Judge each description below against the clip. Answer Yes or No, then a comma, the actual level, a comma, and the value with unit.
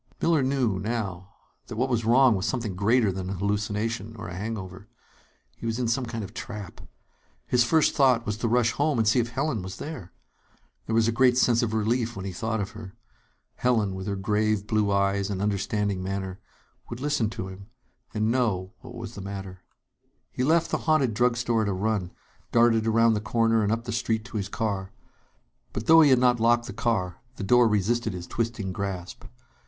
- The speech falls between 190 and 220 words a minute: Yes, fast, 205 wpm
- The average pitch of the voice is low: Yes, low, 110 Hz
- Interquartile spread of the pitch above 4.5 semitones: No, average, 3.3 semitones